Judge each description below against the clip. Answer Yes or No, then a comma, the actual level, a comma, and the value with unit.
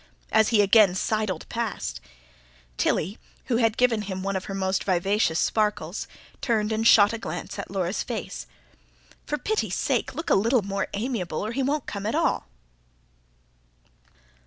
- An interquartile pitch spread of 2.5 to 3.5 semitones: Yes, average, 3.1 semitones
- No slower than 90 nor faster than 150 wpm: No, average, 160 wpm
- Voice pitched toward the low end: No, high, 210 Hz